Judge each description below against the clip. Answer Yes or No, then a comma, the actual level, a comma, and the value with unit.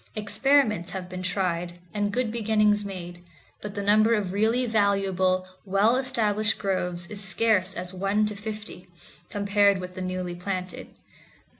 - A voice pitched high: Yes, high, 200 Hz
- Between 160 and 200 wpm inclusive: No, average, 145 wpm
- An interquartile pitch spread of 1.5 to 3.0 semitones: Yes, narrow, 2.5 semitones